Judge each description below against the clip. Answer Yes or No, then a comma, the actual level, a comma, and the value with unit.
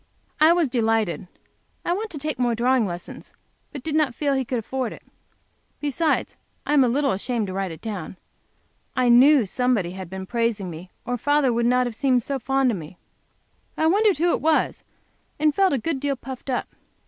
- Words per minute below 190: No, fast, 205 wpm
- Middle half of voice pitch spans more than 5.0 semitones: No, average, 4.6 semitones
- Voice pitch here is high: Yes, very high, 250 Hz